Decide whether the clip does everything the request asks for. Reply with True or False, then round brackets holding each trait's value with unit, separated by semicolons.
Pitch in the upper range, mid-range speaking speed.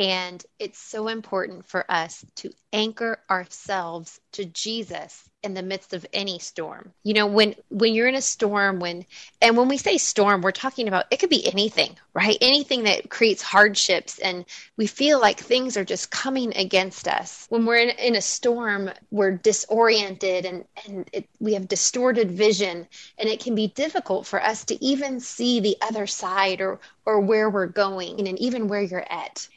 True (210 Hz; 185 wpm)